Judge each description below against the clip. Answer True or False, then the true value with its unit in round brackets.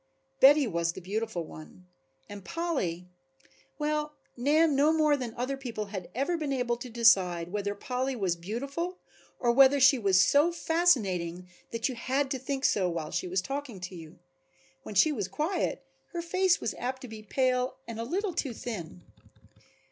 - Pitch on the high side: True (245 Hz)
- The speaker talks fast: False (175 wpm)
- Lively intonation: True (6.9 semitones)